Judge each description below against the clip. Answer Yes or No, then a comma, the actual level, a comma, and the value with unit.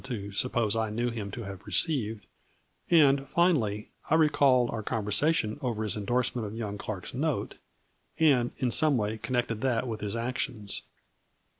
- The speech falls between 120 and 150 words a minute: No, average, 165 wpm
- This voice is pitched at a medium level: No, low, 115 Hz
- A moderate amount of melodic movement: Yes, average, 3.9 semitones